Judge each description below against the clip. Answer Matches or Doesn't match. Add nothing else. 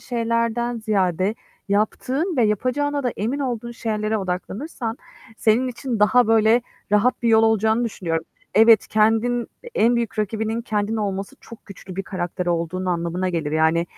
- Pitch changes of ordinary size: Matches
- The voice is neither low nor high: Doesn't match